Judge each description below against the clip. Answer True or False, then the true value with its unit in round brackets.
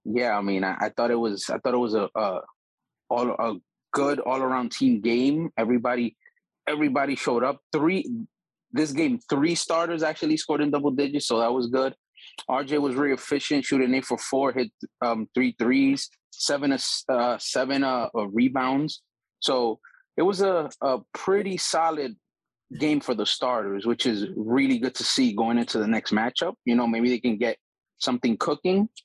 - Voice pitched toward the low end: True (130 Hz)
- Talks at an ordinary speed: True (175 wpm)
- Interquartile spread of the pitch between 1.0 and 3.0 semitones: False (4.3 semitones)